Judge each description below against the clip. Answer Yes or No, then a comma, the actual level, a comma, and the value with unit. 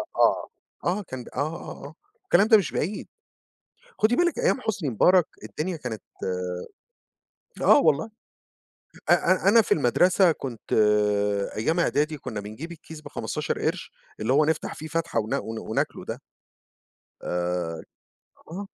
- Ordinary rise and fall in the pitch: No, wide, 7.5 semitones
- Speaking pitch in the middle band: Yes, medium, 155 Hz